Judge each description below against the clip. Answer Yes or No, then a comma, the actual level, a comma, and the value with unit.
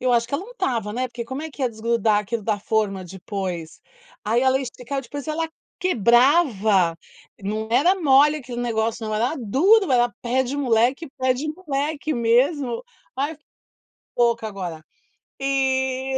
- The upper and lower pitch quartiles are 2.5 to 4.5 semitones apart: Yes, average, 4.1 semitones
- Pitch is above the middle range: Yes, high, 245 Hz